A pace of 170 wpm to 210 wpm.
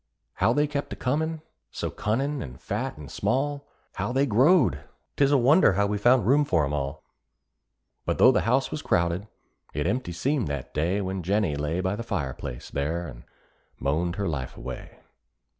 Yes: average, 185 wpm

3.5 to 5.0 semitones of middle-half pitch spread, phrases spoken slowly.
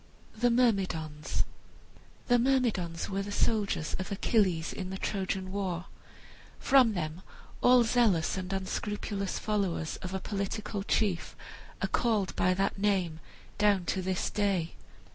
No: average, 2.7 semitones; slow, 130 wpm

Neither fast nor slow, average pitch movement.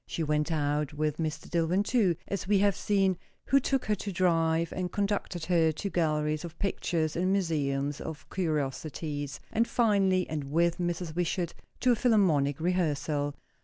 Yes: average, 165 wpm; average, 4.0 semitones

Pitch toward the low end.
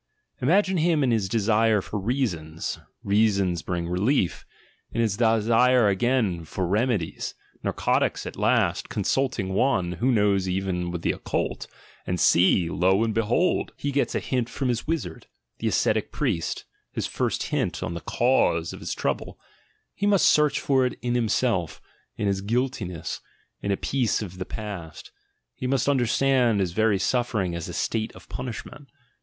Yes: low, 110 Hz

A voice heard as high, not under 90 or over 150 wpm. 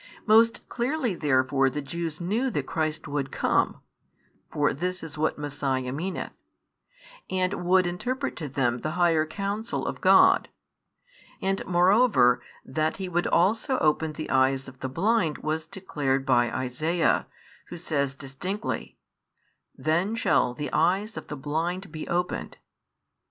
No: medium, 160 Hz; average, 140 wpm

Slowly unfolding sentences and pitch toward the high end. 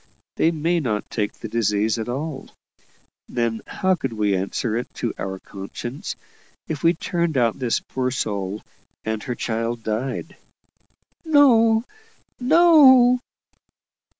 No: slow, 125 wpm; low, 125 Hz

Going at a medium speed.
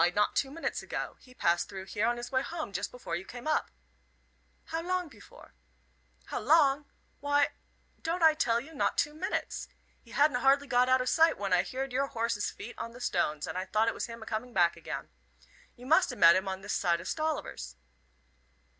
No: fast, 210 wpm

